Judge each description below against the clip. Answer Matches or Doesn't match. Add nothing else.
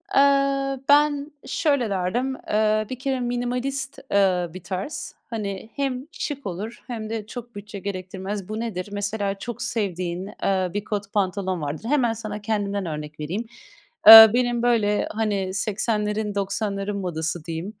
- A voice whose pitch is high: Matches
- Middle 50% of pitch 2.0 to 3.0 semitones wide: Doesn't match